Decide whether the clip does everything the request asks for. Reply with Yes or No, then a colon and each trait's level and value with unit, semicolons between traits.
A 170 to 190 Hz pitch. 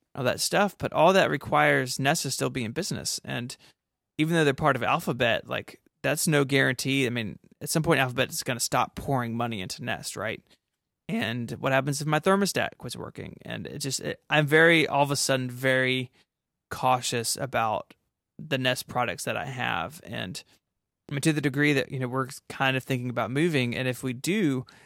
No: low, 135 Hz